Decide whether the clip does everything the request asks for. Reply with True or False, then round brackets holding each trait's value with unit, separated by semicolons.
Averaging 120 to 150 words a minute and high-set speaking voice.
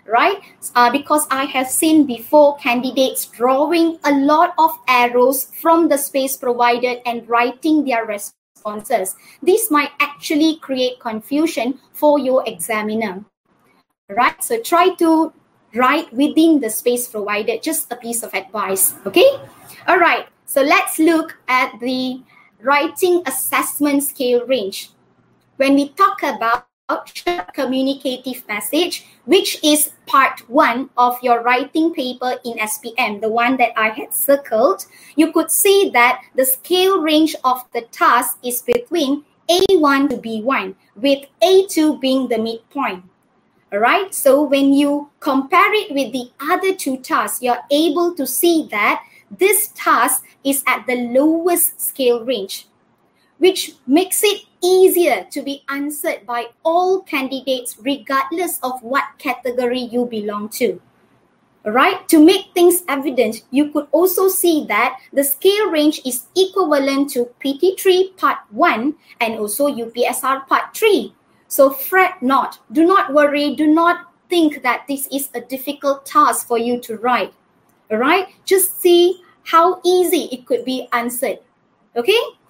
True (140 wpm; 275 Hz)